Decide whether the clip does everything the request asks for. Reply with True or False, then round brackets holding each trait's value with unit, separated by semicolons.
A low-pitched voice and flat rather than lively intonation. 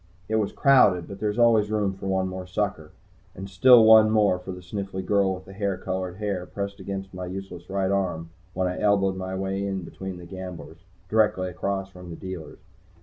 True (95 Hz; 1.6 semitones)